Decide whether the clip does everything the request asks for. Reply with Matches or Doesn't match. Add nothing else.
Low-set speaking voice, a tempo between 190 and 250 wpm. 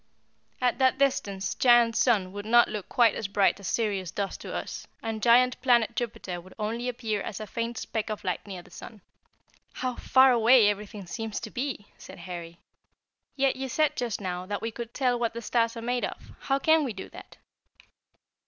Doesn't match